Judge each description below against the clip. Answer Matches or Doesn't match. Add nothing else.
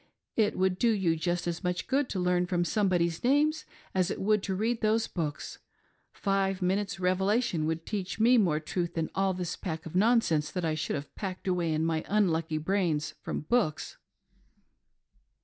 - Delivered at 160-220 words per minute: Matches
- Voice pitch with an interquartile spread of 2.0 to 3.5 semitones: Doesn't match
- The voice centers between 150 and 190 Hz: Matches